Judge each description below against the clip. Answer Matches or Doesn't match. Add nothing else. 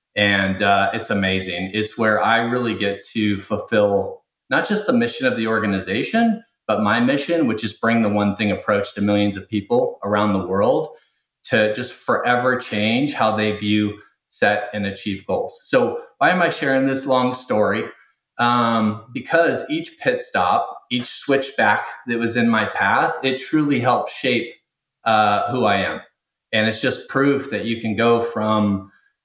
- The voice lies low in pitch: Matches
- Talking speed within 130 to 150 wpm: Doesn't match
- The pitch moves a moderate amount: Matches